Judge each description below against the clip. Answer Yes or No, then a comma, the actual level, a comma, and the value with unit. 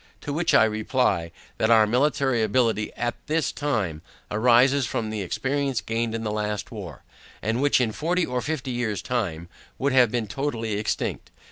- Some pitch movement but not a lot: Yes, average, 3.8 semitones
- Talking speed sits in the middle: Yes, average, 170 wpm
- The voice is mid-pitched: No, low, 115 Hz